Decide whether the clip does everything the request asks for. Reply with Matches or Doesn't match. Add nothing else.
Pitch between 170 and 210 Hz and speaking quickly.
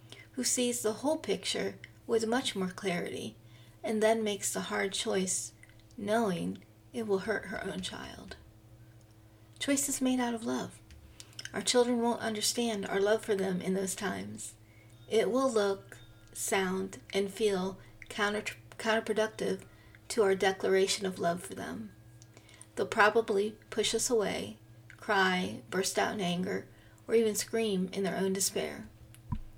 Doesn't match